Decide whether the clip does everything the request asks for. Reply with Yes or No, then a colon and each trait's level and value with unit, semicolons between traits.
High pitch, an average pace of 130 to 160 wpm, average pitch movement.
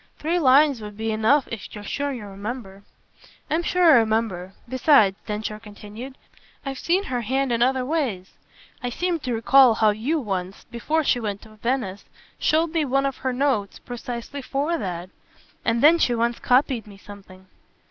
No: high, 240 Hz; average, 175 wpm; average, 4.6 semitones